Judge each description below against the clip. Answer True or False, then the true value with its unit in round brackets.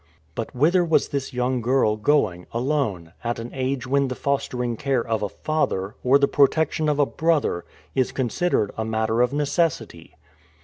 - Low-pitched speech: True (130 Hz)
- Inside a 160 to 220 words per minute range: True (170 wpm)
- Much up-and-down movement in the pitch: False (4.2 semitones)